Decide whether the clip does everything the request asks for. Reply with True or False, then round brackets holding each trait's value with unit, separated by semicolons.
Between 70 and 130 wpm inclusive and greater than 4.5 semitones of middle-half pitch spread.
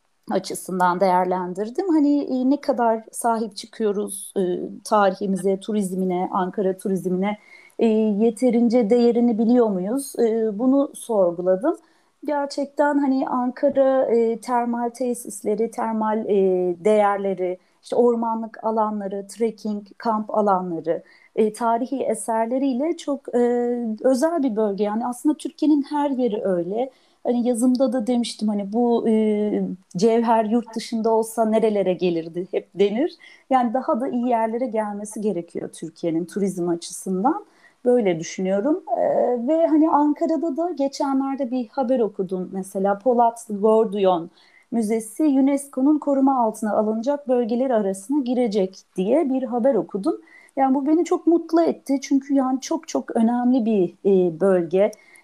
True (125 wpm; 5.0 semitones)